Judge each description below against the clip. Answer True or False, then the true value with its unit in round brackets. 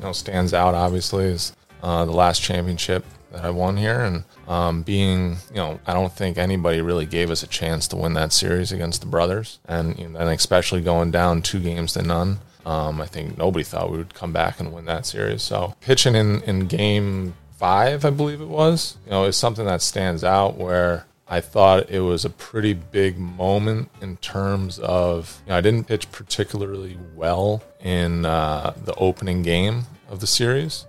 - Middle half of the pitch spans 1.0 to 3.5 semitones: True (2.7 semitones)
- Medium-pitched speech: False (90 Hz)